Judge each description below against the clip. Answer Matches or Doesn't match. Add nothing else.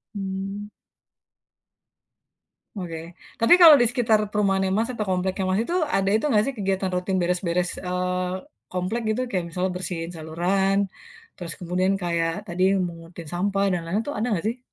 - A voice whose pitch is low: Doesn't match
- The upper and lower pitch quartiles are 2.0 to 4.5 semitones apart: Matches